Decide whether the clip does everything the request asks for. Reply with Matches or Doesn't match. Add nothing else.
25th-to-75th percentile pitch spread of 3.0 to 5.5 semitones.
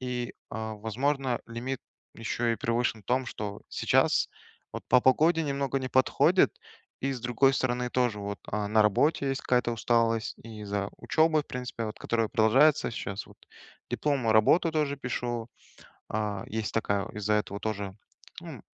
Matches